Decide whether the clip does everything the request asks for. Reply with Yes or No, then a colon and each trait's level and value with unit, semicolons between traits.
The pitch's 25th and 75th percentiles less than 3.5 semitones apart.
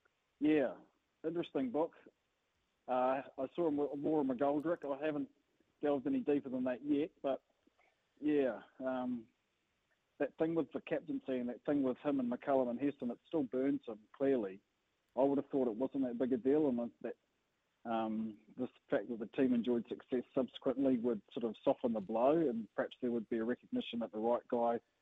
Yes: average, 3.0 semitones